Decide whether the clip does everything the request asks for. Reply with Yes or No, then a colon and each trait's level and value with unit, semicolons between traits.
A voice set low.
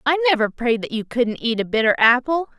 No: very high, 250 Hz